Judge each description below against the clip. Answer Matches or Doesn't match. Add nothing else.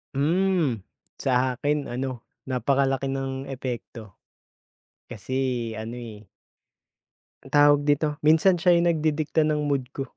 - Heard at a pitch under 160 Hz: Matches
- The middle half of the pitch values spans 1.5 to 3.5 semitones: Matches